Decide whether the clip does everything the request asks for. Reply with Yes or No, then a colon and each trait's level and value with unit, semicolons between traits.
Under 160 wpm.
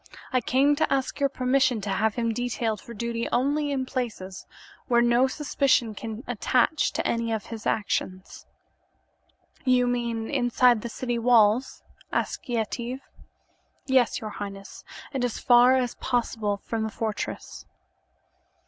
Yes: average, 140 wpm